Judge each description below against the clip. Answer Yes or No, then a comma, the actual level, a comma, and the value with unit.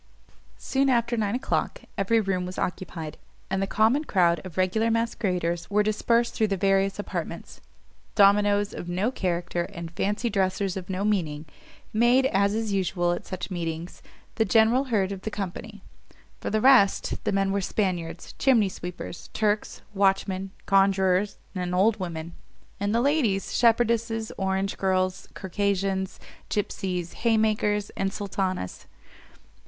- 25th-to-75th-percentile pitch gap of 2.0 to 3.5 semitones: Yes, average, 2.8 semitones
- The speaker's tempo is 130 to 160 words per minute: Yes, average, 140 wpm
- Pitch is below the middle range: No, high, 195 Hz